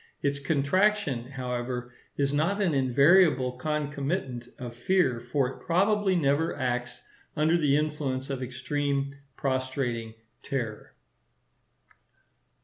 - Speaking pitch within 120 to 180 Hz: Yes, medium, 140 Hz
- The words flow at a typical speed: No, slow, 105 wpm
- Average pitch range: Yes, average, 3.4 semitones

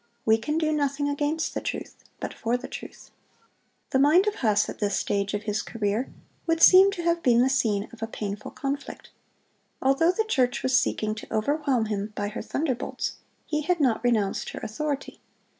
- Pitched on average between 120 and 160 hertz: No, very high, 260 Hz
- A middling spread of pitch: No, wide, 5.8 semitones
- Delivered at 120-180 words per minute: No, average, 190 wpm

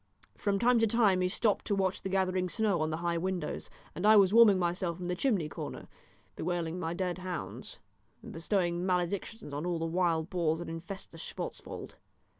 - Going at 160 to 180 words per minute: No, average, 195 wpm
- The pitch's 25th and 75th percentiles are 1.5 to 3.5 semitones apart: Yes, narrow, 2.5 semitones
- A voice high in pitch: No, medium, 180 Hz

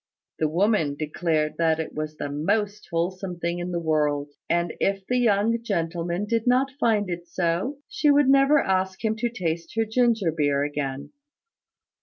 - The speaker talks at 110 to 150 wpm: No, average, 170 wpm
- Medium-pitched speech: Yes, medium, 180 Hz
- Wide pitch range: Yes, wide, 5.7 semitones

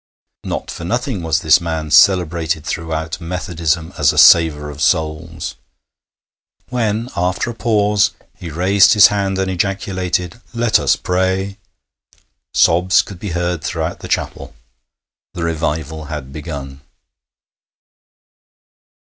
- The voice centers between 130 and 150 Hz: No, very low, 85 Hz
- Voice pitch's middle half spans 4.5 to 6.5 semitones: No, average, 3.2 semitones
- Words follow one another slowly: Yes, slow, 120 wpm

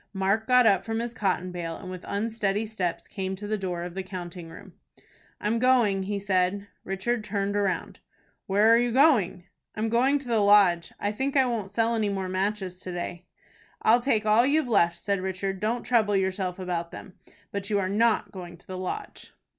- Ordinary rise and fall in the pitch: Yes, average, 3.2 semitones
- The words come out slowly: No, average, 200 wpm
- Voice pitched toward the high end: Yes, high, 200 Hz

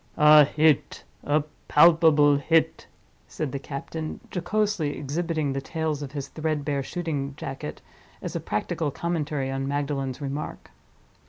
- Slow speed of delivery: Yes, slow, 120 wpm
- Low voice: No, medium, 150 Hz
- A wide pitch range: No, narrow, 2.5 semitones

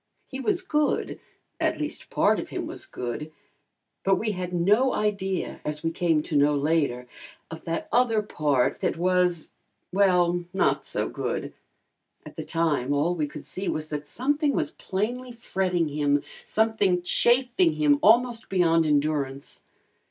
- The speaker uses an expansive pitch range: Yes, wide, 6.1 semitones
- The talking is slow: No, average, 150 wpm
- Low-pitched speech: No, medium, 175 Hz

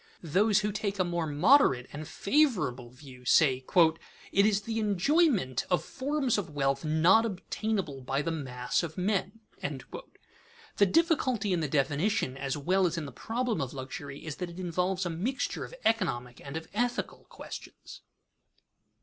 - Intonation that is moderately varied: No, wide, 7.1 semitones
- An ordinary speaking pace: Yes, average, 160 wpm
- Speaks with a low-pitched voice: No, medium, 180 Hz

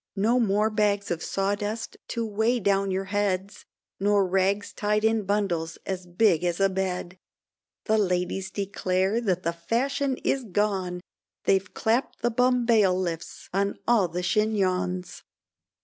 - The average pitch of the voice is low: No, high, 200 Hz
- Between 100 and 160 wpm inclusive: Yes, slow, 135 wpm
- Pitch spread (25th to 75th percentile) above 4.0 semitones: No, average, 2.8 semitones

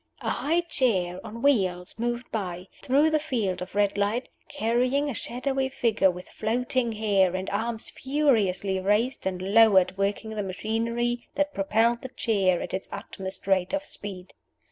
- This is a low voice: No, high, 220 Hz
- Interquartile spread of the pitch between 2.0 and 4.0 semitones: No, average, 4.6 semitones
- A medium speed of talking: Yes, average, 160 wpm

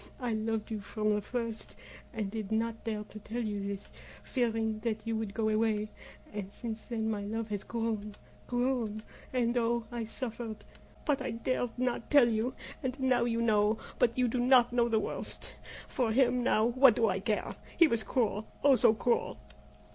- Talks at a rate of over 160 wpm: Yes, average, 185 wpm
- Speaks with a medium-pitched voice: No, high, 225 Hz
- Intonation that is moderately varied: No, narrow, 2.1 semitones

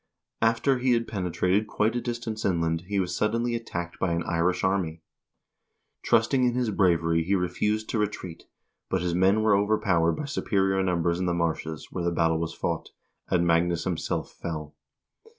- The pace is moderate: Yes, average, 175 wpm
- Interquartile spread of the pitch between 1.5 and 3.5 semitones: No, average, 4.3 semitones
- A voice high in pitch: No, very low, 95 Hz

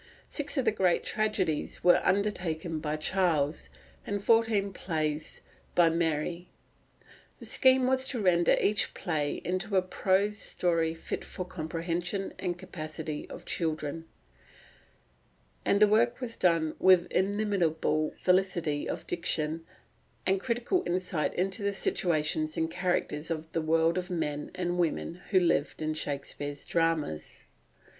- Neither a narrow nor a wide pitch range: Yes, average, 3.5 semitones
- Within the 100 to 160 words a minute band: Yes, slow, 135 wpm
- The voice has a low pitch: No, medium, 175 Hz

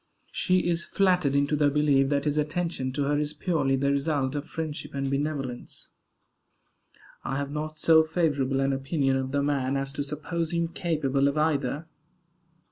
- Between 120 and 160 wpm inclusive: No, average, 170 wpm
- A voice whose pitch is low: No, medium, 145 Hz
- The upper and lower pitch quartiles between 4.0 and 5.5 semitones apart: No, narrow, 2.4 semitones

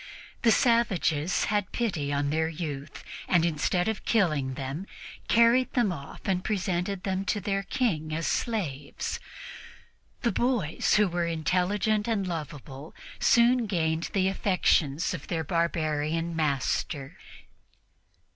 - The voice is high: No, medium, 175 Hz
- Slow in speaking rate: Yes, slow, 125 wpm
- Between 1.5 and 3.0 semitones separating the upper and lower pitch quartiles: No, average, 5.1 semitones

